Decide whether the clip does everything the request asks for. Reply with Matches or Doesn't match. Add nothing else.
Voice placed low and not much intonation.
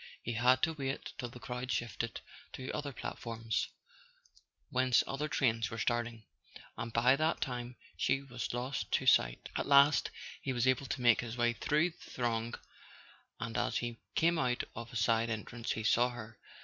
Matches